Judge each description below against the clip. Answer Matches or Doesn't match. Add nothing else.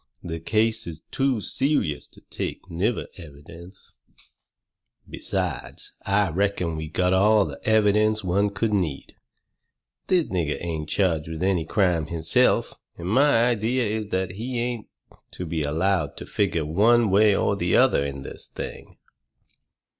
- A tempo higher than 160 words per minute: Doesn't match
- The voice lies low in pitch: Matches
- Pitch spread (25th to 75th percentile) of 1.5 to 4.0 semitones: Doesn't match